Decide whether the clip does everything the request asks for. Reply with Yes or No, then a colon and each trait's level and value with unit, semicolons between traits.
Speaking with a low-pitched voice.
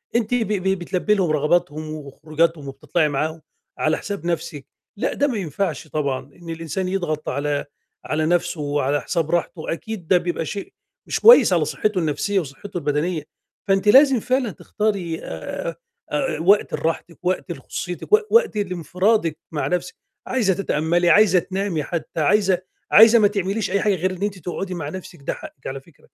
No: medium, 175 Hz